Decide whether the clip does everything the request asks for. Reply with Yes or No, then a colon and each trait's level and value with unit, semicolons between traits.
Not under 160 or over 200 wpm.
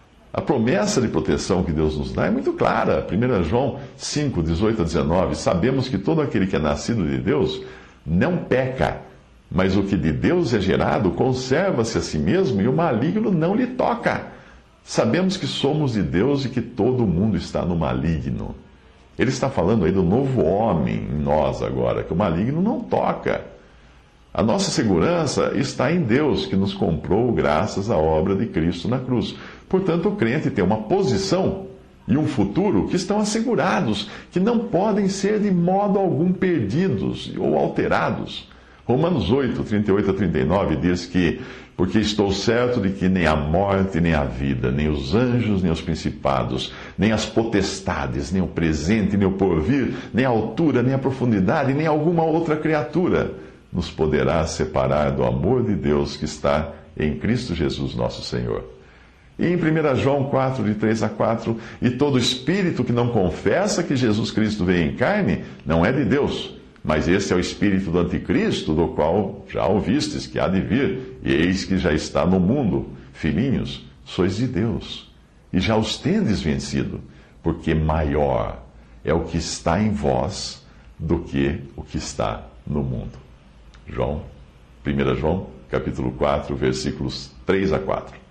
Yes: average, 170 wpm